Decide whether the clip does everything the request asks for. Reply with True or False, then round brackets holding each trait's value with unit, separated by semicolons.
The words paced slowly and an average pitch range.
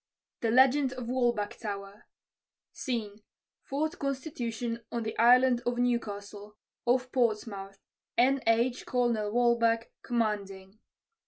True (105 wpm; 3.0 semitones)